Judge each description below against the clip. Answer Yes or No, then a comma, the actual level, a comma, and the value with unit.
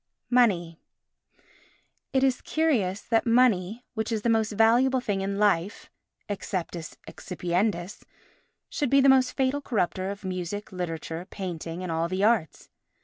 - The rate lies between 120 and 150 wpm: Yes, average, 140 wpm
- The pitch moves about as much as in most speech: Yes, average, 5.0 semitones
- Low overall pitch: No, high, 205 Hz